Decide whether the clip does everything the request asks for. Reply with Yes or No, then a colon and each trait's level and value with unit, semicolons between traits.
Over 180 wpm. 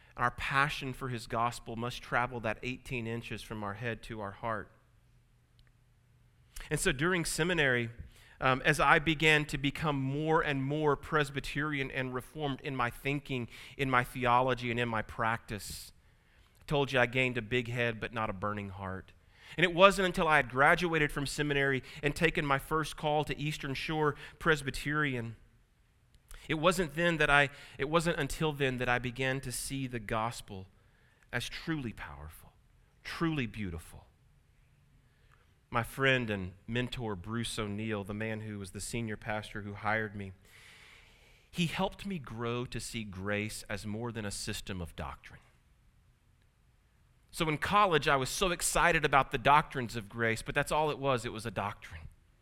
No: average, 165 wpm